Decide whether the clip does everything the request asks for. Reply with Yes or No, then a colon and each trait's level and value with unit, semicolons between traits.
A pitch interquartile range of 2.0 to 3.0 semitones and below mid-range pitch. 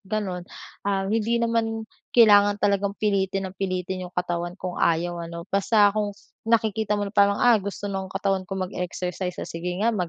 No: narrow, 2.6 semitones; high, 200 Hz